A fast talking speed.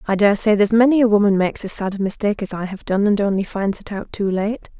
Yes: fast, 290 wpm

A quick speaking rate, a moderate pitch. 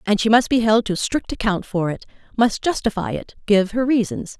No: fast, 220 wpm; high, 215 Hz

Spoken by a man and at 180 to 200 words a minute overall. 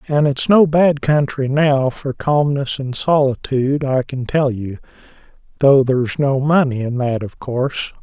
No: male; average, 155 wpm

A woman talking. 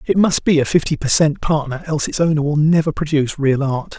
No: male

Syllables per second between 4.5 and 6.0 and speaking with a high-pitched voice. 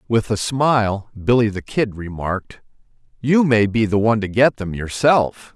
No: 4.6 syllables/s; low, 110 Hz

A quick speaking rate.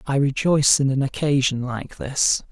No: average, 165 wpm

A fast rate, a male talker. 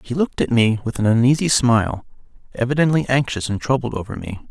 No: average, 185 wpm; male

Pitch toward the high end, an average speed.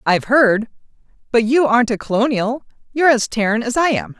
Yes: high, 240 Hz; average, 170 wpm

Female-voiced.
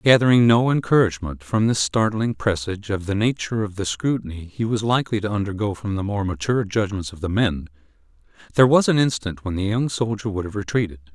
No: male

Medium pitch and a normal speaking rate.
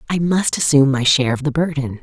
No: medium, 145 Hz; fast, 235 wpm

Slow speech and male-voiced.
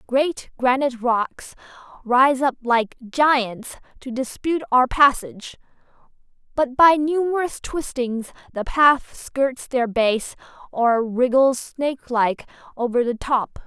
No: slow, 115 wpm; female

